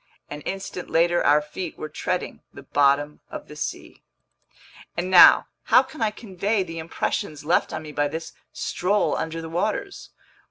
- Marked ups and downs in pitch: No, average, 3.7 semitones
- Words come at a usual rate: Yes, average, 165 wpm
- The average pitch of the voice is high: No, medium, 165 Hz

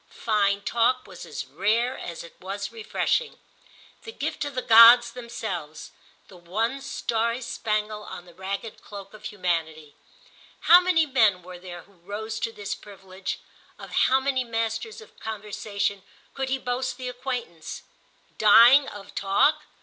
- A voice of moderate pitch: No, high, 220 Hz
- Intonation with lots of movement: No, average, 4.2 semitones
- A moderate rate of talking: Yes, average, 145 wpm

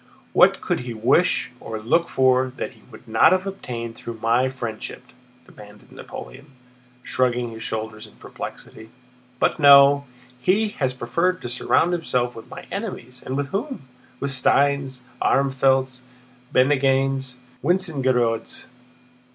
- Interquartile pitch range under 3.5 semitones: Yes, average, 3.1 semitones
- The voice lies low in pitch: Yes, low, 130 Hz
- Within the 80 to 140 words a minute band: Yes, slow, 135 wpm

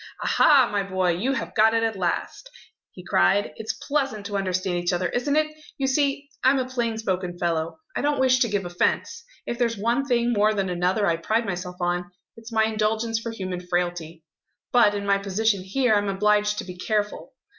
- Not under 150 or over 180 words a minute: No, average, 200 wpm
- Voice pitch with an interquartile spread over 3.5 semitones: Yes, average, 4.5 semitones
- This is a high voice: Yes, high, 210 Hz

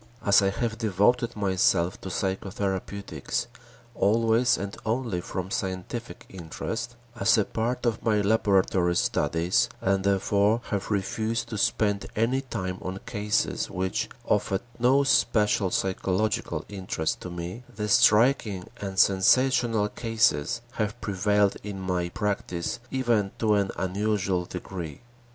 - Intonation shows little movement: No, average, 3.1 semitones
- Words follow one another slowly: Yes, slow, 125 wpm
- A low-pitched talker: Yes, low, 100 Hz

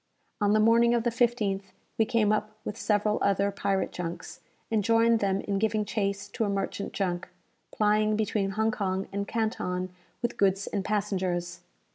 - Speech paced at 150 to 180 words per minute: Yes, average, 170 wpm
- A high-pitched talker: Yes, high, 205 Hz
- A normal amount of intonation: No, narrow, 2.0 semitones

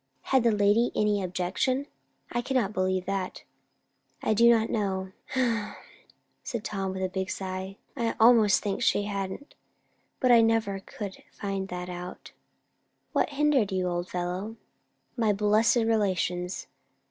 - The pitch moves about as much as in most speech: Yes, average, 3.2 semitones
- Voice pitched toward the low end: No, high, 205 Hz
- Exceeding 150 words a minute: No, slow, 135 wpm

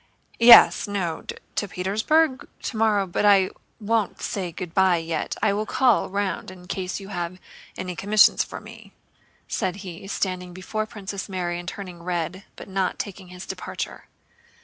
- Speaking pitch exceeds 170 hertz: Yes, high, 190 Hz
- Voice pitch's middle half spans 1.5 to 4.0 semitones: Yes, narrow, 2.4 semitones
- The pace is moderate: Yes, average, 150 wpm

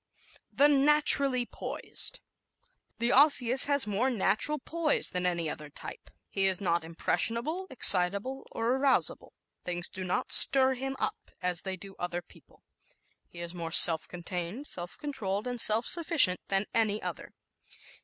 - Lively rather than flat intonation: Yes, wide, 7.1 semitones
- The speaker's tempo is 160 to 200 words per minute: No, average, 150 wpm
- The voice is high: Yes, high, 215 Hz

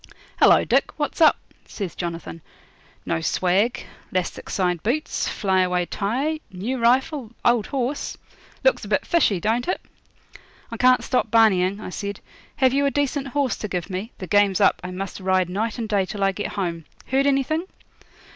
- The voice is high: Yes, high, 215 Hz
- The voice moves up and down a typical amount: No, wide, 6.0 semitones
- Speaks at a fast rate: No, average, 170 wpm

